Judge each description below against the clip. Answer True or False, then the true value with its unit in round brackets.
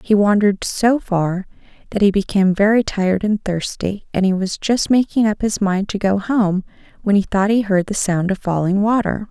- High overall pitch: True (200 Hz)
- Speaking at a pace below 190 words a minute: False (205 wpm)